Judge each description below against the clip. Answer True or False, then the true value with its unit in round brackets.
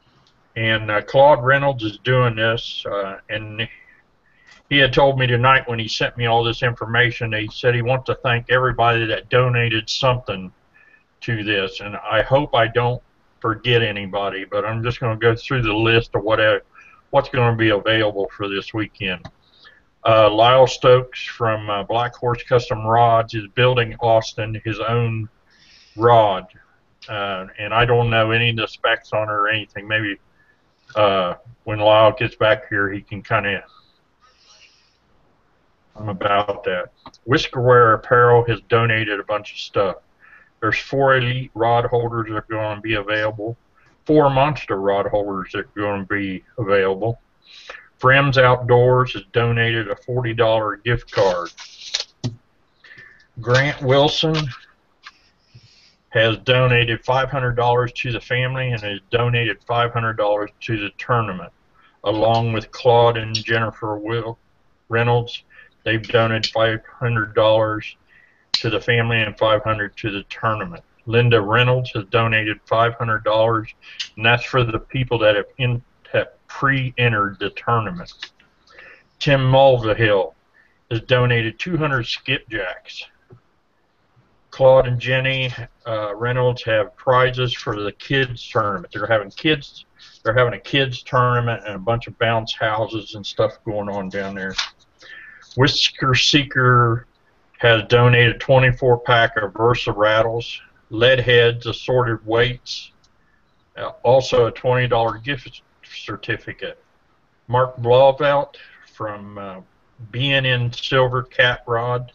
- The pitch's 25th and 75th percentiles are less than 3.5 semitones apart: True (2.5 semitones)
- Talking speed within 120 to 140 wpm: True (135 wpm)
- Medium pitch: False (115 Hz)